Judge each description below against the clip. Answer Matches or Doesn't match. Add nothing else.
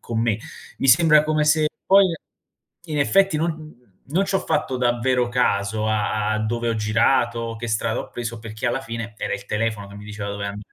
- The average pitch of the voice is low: Matches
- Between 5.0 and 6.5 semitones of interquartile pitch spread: Matches